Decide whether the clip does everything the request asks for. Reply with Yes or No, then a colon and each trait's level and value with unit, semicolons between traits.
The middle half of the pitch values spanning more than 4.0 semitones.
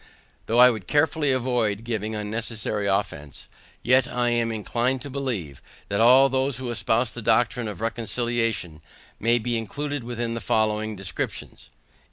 No: narrow, 2.6 semitones